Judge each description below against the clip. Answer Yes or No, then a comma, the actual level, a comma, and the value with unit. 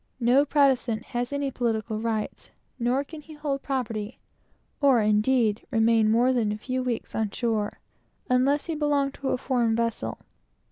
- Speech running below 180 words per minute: Yes, average, 155 wpm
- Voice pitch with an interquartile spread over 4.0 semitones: No, average, 3.7 semitones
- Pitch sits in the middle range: No, high, 245 Hz